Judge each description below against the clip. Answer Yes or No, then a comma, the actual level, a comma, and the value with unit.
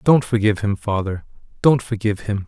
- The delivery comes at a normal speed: Yes, average, 170 wpm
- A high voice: No, low, 105 Hz